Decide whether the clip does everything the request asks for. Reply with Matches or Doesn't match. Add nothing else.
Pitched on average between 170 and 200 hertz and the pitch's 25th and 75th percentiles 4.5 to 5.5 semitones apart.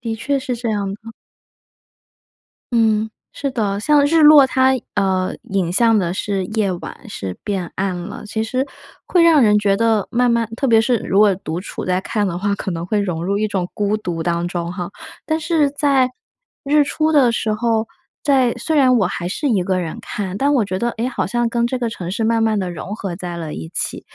Doesn't match